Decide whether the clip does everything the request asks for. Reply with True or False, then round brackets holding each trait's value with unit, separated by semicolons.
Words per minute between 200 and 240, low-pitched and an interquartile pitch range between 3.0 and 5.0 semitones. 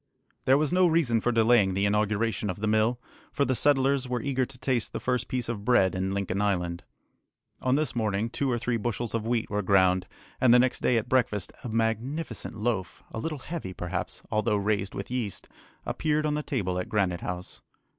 True (205 wpm; 115 Hz; 4.2 semitones)